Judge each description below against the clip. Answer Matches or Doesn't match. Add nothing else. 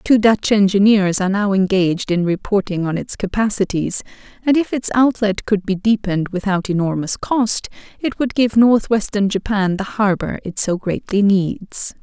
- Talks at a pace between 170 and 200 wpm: Doesn't match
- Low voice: Doesn't match